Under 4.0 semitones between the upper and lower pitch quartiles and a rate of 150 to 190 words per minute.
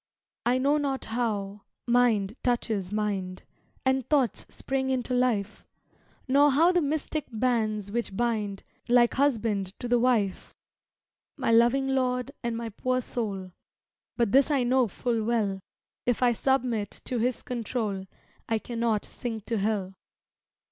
No: average, 3.2 semitones; average, 140 wpm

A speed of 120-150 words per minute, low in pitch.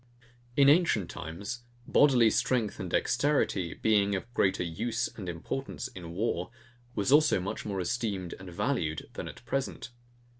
Yes: average, 145 wpm; low, 105 Hz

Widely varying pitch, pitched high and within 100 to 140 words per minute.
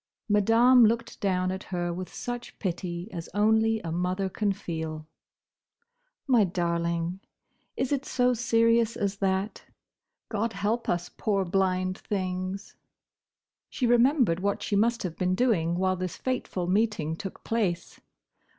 No: average, 4.1 semitones; high, 195 Hz; slow, 135 wpm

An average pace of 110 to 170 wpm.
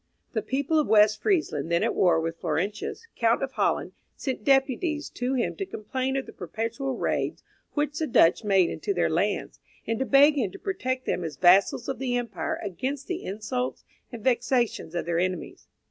No: average, 190 wpm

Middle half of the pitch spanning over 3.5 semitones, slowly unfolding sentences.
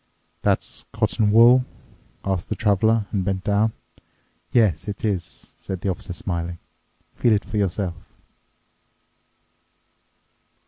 No: average, 3.0 semitones; slow, 110 wpm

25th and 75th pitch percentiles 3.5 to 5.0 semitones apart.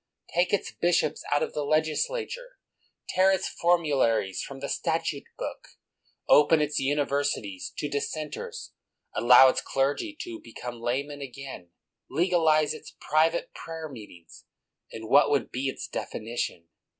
Yes: average, 3.8 semitones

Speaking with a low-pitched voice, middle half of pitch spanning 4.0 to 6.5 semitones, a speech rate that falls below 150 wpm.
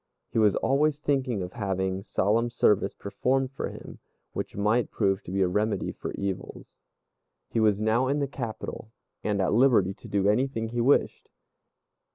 No: low, 110 Hz; average, 4.3 semitones; average, 170 wpm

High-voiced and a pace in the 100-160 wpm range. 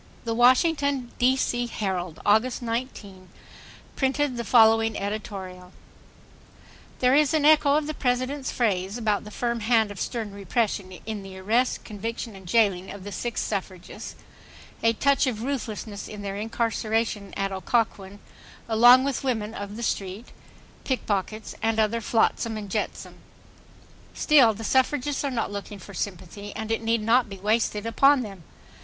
Yes: high, 225 Hz; average, 150 wpm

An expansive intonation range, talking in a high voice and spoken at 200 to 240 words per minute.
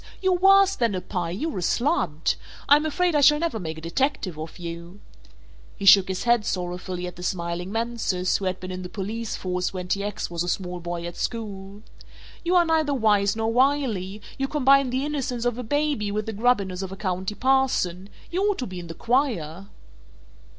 Yes: wide, 6.7 semitones; high, 205 Hz; fast, 205 wpm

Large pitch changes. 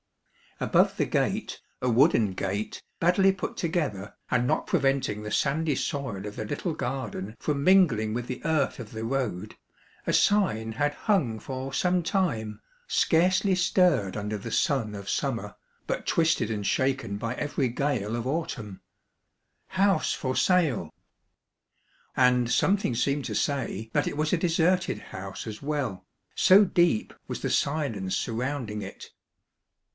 Yes: wide, 6.9 semitones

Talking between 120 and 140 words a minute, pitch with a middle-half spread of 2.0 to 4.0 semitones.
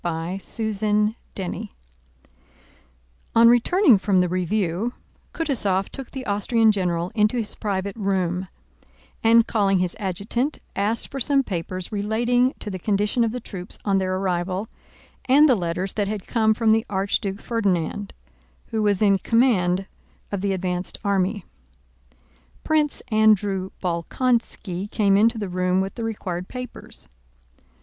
Yes: slow, 135 wpm; average, 3.4 semitones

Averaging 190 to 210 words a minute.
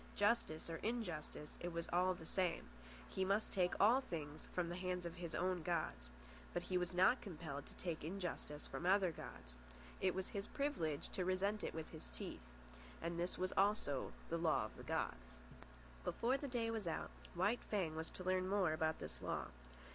Yes: average, 195 wpm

